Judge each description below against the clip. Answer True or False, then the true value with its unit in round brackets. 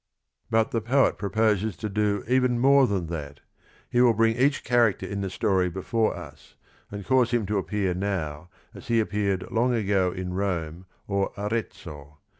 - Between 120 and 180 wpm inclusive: True (170 wpm)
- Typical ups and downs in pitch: True (3.8 semitones)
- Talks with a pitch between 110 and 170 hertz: False (100 Hz)